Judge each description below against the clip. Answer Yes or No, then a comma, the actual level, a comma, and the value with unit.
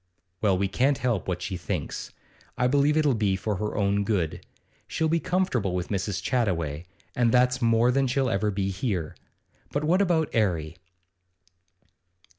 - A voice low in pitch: Yes, low, 110 Hz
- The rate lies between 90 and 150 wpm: No, average, 160 wpm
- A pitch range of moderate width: No, wide, 5.8 semitones